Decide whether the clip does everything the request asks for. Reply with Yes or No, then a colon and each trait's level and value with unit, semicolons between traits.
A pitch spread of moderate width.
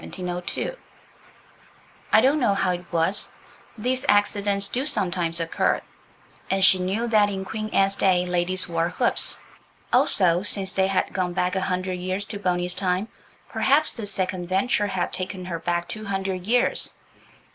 No: narrow, 2.2 semitones